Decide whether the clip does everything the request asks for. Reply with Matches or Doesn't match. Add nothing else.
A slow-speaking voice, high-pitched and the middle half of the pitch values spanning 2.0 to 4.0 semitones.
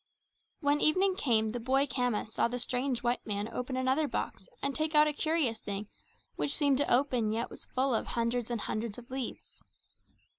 Doesn't match